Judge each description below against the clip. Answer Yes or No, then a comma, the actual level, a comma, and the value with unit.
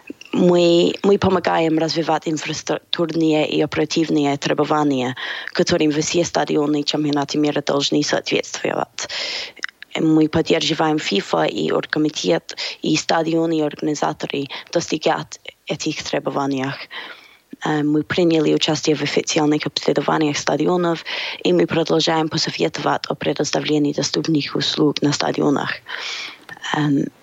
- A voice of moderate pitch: Yes, medium, 155 Hz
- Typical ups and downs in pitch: No, narrow, 1.9 semitones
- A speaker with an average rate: No, slow, 105 wpm